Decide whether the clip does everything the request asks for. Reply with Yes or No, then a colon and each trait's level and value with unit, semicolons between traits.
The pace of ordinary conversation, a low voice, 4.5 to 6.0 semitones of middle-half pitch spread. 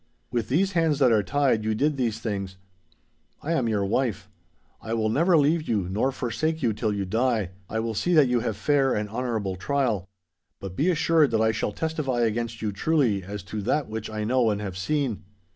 No: fast, 210 wpm; low, 115 Hz; average, 5.2 semitones